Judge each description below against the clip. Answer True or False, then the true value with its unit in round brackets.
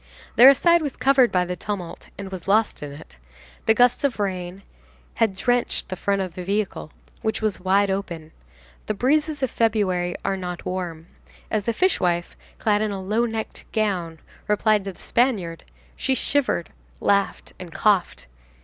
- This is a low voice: False (200 Hz)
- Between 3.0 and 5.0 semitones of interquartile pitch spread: True (4.0 semitones)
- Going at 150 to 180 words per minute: True (165 wpm)